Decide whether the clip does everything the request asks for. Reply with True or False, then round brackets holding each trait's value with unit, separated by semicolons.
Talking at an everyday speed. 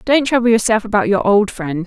False (225 wpm)